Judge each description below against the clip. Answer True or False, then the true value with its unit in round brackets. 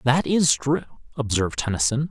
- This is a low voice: True (130 Hz)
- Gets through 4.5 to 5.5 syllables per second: True (5.4 syllables/s)